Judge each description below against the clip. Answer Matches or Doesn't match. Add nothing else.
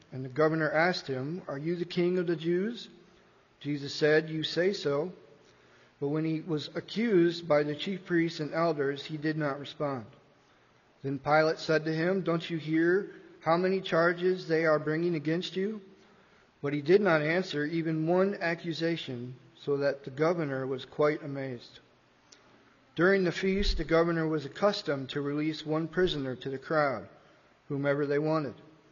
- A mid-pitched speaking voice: Matches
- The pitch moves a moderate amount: Matches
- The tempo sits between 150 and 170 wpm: Matches